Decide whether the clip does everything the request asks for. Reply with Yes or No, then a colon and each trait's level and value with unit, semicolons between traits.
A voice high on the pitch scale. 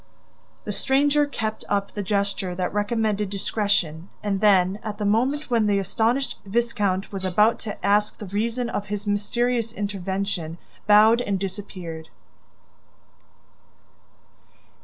Yes: high, 205 Hz